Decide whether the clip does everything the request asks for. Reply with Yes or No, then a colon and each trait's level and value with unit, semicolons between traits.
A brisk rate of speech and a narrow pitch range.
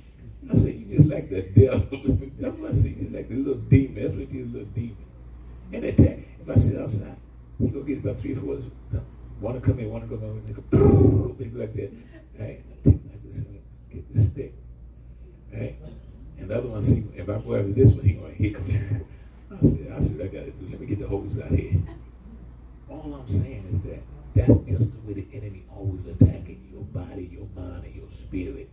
No: fast, 235 wpm; average, 3.6 semitones